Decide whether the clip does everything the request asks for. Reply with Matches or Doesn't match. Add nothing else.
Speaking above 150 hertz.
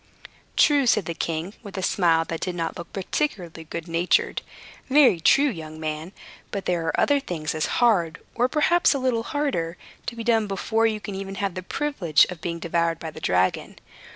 Matches